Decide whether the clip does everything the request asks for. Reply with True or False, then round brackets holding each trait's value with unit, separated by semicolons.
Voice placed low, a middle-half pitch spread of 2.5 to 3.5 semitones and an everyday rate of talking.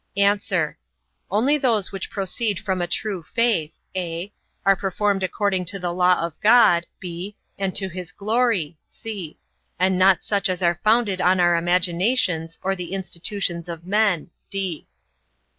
False (185 Hz; 2.9 semitones; 145 wpm)